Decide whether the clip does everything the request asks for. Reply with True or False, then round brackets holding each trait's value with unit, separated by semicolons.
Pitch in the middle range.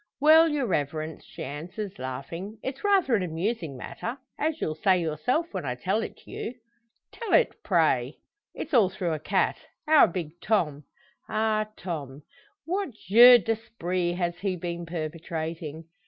True (180 Hz)